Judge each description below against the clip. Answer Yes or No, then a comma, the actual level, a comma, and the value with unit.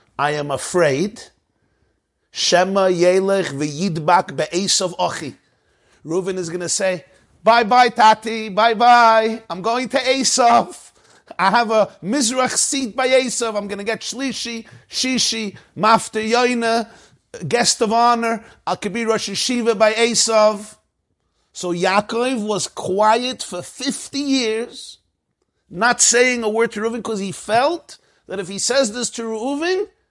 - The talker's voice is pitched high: Yes, high, 225 Hz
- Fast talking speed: No, slow, 135 wpm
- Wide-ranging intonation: No, average, 3.7 semitones